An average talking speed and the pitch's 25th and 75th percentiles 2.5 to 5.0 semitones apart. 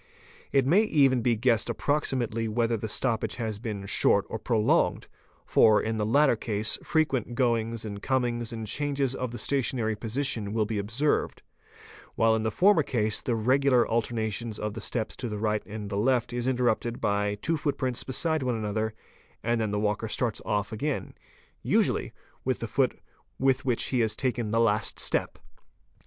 Yes: average, 175 wpm; average, 3.1 semitones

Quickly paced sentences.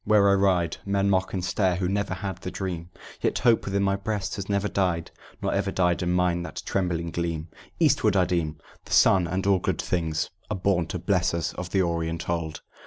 Yes: fast, 215 wpm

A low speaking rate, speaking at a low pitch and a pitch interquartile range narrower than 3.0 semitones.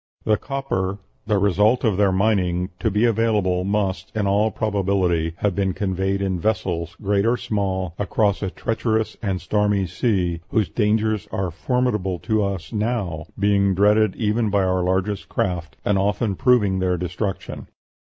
No: average, 155 wpm; low, 100 Hz; narrow, 2.5 semitones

